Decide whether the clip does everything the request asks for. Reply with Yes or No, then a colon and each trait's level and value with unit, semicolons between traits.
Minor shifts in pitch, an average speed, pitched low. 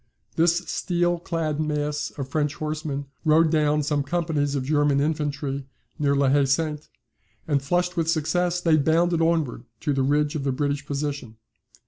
No: narrow, 2.3 semitones; average, 160 wpm; medium, 150 Hz